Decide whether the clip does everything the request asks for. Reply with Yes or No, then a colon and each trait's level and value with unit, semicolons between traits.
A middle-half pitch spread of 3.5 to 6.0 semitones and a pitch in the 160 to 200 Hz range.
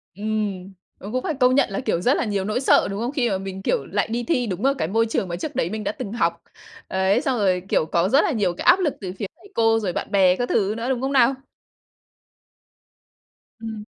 No: average, 4.7 semitones; high, 215 Hz